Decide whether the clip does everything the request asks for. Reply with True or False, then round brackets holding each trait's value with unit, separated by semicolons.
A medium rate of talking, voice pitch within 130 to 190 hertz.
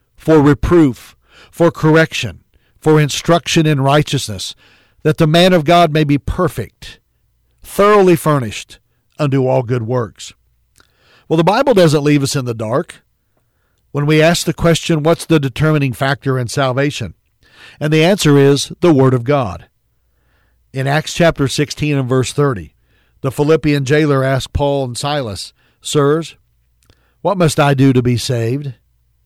True (150 wpm; 140 Hz)